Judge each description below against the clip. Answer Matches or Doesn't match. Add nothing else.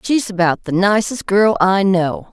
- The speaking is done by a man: Doesn't match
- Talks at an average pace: Matches